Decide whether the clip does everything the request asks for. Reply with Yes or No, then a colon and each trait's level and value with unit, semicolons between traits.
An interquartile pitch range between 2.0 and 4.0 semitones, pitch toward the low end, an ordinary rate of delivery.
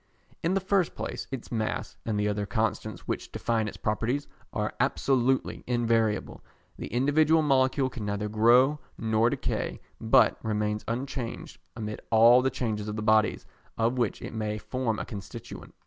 Yes: average, 3.3 semitones; low, 115 Hz; average, 160 wpm